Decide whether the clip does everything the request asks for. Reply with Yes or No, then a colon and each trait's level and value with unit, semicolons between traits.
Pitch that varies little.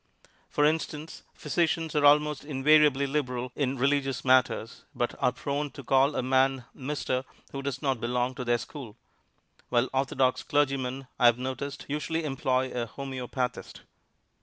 Yes: narrow, 2.3 semitones